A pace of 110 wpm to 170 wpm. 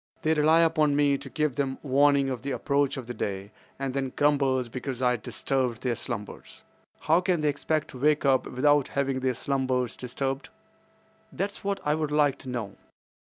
No: average, 180 wpm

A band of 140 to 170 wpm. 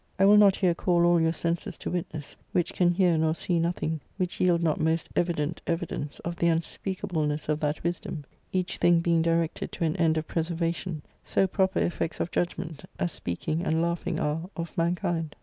No: average, 200 wpm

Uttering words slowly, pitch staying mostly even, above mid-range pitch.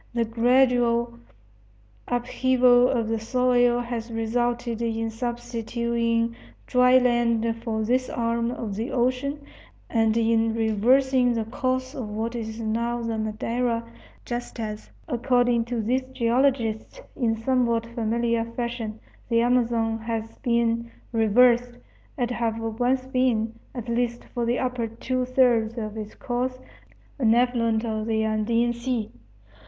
Yes: slow, 130 wpm; narrow, 1.5 semitones; high, 235 Hz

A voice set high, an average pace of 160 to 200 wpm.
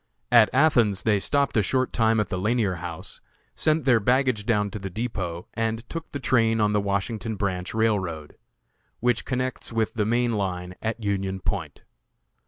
No: low, 110 Hz; average, 175 wpm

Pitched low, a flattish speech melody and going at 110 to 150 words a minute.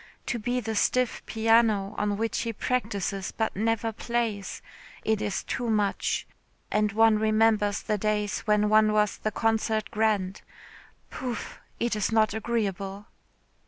No: high, 215 Hz; narrow, 1.5 semitones; average, 140 wpm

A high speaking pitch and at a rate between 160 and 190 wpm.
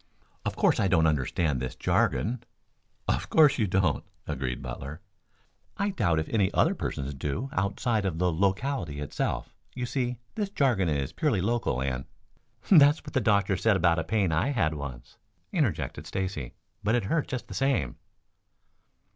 No: very low, 95 Hz; average, 165 wpm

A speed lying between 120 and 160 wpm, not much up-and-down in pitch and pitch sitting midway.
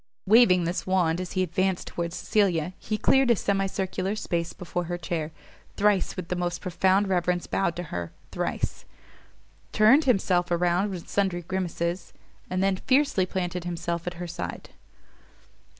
Yes: average, 155 wpm; narrow, 2.0 semitones; medium, 180 Hz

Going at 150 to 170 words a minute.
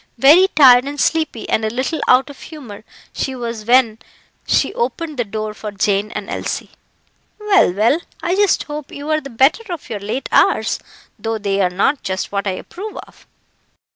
No: average, 180 wpm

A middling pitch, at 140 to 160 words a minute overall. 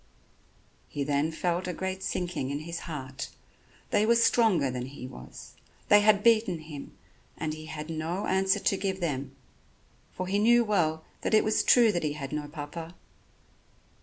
No: medium, 170 Hz; average, 170 wpm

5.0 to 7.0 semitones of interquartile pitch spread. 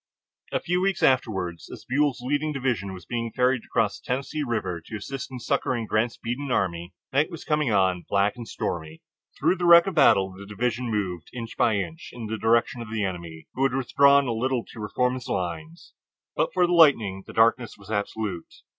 Yes: average, 5.3 semitones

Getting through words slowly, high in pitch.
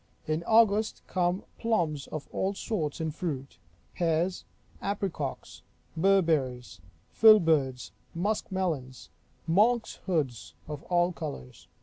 No: slow, 100 wpm; medium, 165 Hz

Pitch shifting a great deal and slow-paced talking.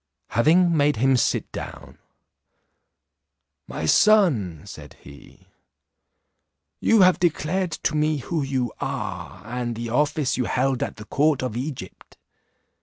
No: average, 4.9 semitones; slow, 125 wpm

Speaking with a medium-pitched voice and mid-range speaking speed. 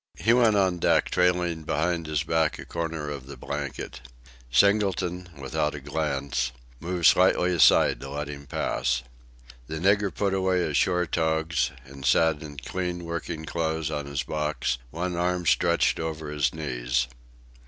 No: very low, 80 Hz; average, 155 wpm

